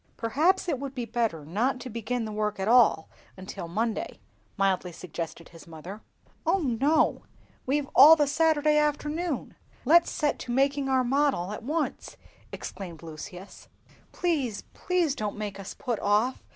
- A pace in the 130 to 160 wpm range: Yes, average, 150 wpm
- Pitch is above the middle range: Yes, high, 245 Hz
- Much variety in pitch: Yes, wide, 6.6 semitones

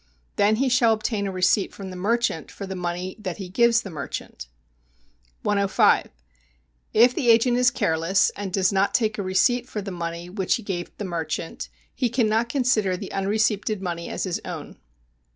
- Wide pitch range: No, average, 3.8 semitones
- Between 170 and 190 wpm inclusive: Yes, average, 180 wpm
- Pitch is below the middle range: No, high, 200 Hz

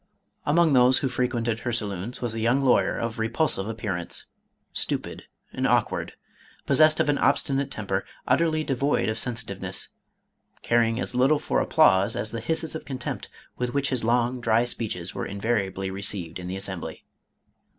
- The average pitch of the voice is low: Yes, low, 120 Hz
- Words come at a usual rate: Yes, average, 160 wpm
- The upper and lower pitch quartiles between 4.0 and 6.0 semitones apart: Yes, average, 4.3 semitones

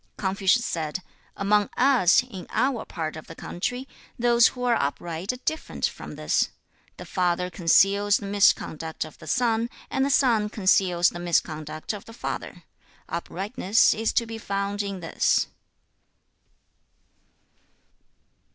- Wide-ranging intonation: No, average, 4.9 semitones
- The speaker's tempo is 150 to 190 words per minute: No, average, 140 wpm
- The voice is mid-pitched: No, high, 200 Hz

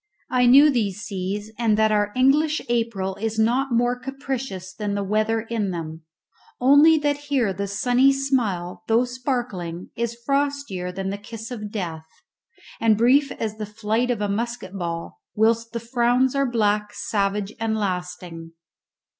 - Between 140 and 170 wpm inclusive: Yes, average, 155 wpm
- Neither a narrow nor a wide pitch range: Yes, average, 3.8 semitones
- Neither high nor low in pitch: No, high, 225 Hz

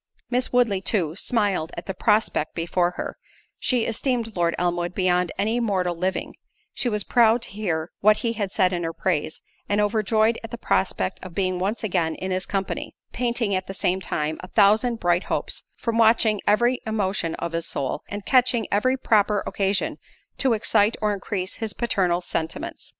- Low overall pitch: No, high, 200 Hz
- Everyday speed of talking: Yes, average, 175 wpm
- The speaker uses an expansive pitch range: No, average, 3.9 semitones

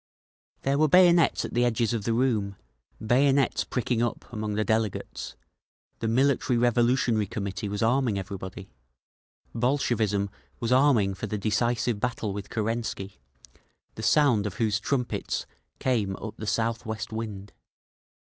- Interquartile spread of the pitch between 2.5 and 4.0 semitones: Yes, average, 3.0 semitones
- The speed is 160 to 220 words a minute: No, average, 140 wpm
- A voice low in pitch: Yes, low, 115 Hz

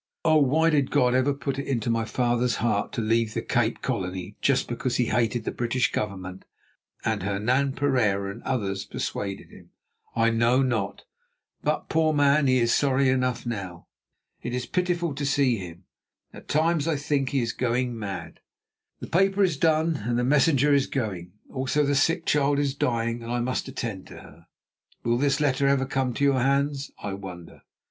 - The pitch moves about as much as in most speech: Yes, average, 3.7 semitones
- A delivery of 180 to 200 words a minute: Yes, average, 185 wpm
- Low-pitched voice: Yes, low, 125 Hz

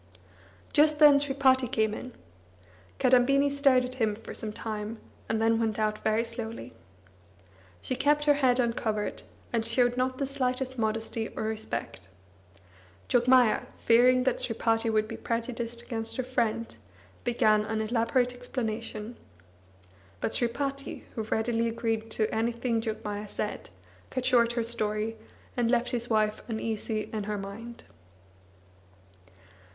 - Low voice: No, high, 230 Hz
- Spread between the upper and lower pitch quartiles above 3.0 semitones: No, narrow, 2.5 semitones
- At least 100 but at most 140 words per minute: Yes, slow, 135 wpm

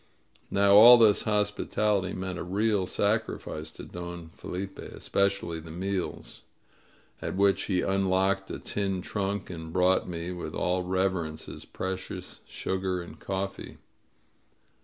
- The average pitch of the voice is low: Yes, very low, 95 Hz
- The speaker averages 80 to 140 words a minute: Yes, slow, 135 wpm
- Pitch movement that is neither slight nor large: No, narrow, 1.8 semitones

